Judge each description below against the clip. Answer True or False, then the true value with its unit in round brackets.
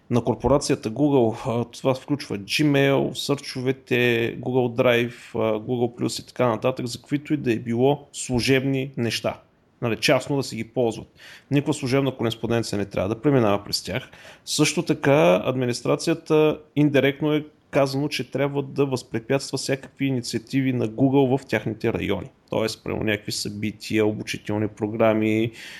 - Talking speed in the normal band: True (140 wpm)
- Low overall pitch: True (130 Hz)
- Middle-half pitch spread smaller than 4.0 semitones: True (3.6 semitones)